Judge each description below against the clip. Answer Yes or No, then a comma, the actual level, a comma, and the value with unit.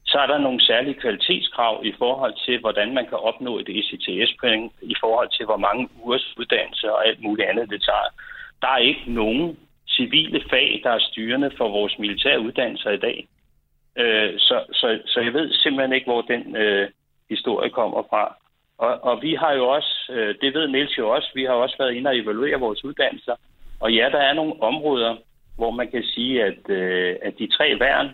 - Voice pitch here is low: Yes, low, 115 Hz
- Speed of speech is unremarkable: Yes, average, 200 wpm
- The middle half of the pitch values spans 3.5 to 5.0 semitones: Yes, average, 4.3 semitones